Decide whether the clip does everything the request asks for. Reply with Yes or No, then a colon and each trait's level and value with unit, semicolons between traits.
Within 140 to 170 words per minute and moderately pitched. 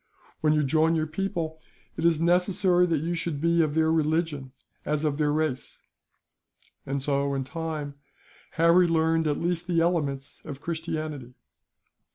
Yes: average, 160 wpm; medium, 160 Hz